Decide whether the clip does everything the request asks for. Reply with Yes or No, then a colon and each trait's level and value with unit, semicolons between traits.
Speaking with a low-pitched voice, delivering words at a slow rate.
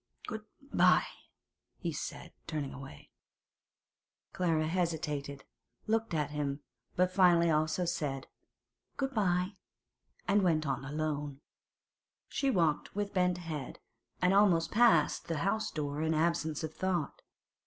No: medium, 165 Hz; slow, 120 wpm